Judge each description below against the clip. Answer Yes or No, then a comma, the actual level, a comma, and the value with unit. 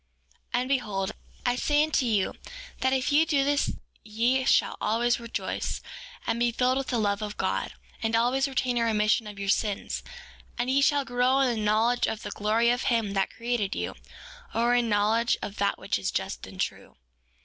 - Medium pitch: No, high, 235 Hz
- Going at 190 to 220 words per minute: Yes, average, 200 wpm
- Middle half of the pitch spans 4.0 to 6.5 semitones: No, average, 3.2 semitones